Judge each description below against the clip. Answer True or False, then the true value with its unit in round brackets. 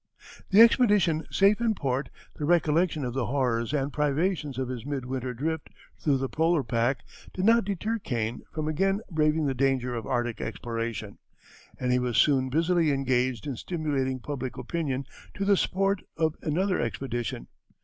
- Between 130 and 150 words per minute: False (165 wpm)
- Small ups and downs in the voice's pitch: False (5.0 semitones)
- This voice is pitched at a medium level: True (145 Hz)